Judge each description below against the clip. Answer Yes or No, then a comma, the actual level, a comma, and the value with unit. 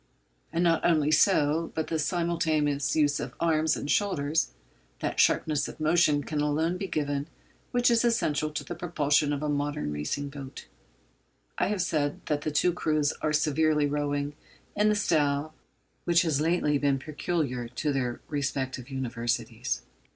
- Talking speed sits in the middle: Yes, average, 160 wpm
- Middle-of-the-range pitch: Yes, medium, 150 Hz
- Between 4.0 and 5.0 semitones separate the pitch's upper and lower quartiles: No, narrow, 2.4 semitones